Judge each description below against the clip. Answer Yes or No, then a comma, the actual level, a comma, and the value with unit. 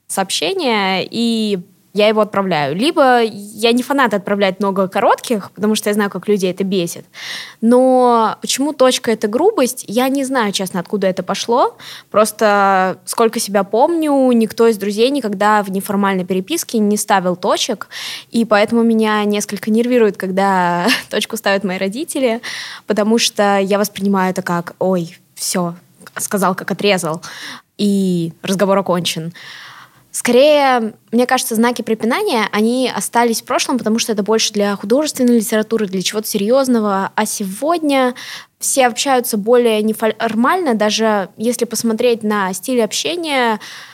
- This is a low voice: No, high, 215 Hz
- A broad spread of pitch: No, average, 3.3 semitones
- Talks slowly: No, average, 140 wpm